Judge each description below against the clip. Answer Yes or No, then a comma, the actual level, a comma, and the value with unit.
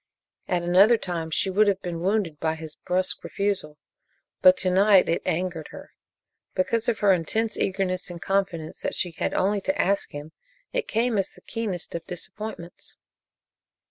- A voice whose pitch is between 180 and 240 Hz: Yes, medium, 185 Hz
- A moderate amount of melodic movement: Yes, average, 3.3 semitones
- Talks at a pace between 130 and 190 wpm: Yes, average, 170 wpm